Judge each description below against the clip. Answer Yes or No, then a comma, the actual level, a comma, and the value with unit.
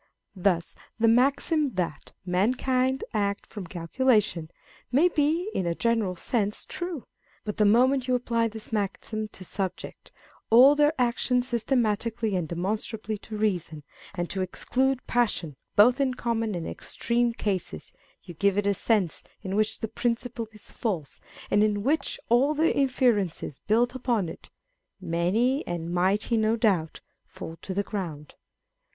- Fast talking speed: No, average, 155 wpm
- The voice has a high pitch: Yes, high, 220 Hz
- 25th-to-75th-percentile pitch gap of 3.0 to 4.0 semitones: No, average, 4.7 semitones